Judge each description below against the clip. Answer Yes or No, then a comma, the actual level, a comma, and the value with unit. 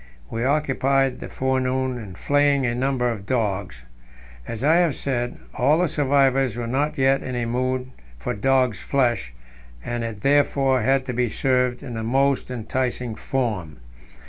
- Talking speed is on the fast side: No, average, 160 wpm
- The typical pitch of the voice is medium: No, low, 130 Hz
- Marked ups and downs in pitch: No, narrow, 2.4 semitones